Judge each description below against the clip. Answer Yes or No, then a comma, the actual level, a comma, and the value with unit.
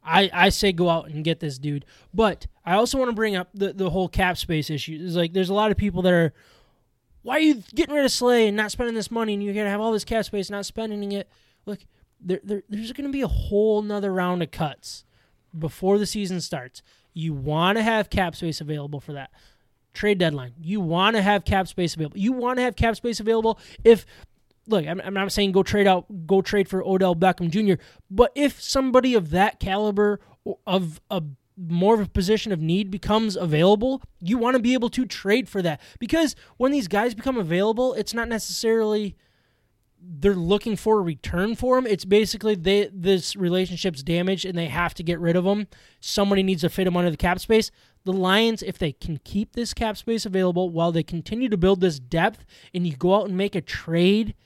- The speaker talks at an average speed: No, fast, 220 wpm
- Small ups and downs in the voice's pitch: No, average, 3.9 semitones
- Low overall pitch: No, high, 195 Hz